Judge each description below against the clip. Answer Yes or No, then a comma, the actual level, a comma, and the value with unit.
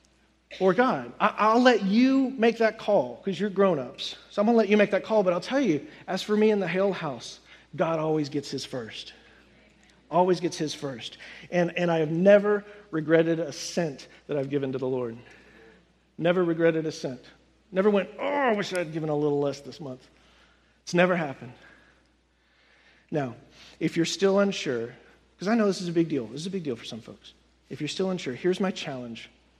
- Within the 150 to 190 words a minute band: No, fast, 205 wpm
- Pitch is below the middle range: No, medium, 175 Hz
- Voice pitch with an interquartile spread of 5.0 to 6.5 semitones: Yes, wide, 5.5 semitones